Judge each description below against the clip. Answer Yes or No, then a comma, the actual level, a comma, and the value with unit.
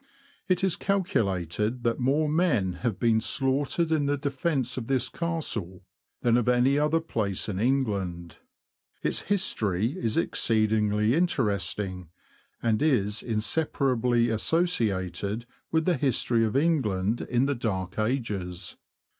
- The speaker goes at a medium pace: No, slow, 125 wpm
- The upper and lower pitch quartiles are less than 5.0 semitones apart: No, wide, 5.6 semitones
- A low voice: Yes, low, 120 Hz